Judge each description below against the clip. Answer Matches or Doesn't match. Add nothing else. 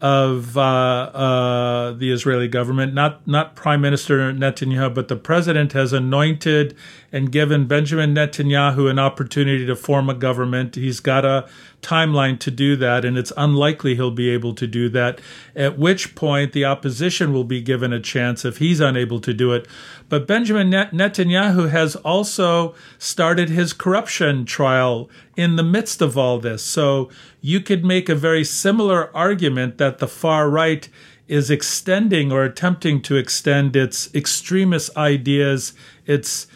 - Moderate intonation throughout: Matches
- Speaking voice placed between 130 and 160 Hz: Matches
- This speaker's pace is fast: Doesn't match